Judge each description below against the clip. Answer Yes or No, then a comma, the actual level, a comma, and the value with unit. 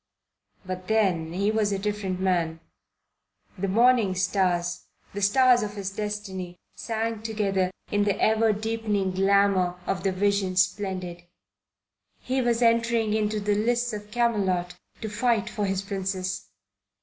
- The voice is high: Yes, high, 200 Hz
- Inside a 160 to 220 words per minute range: No, slow, 135 wpm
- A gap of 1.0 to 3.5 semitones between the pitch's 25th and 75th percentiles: Yes, average, 2.8 semitones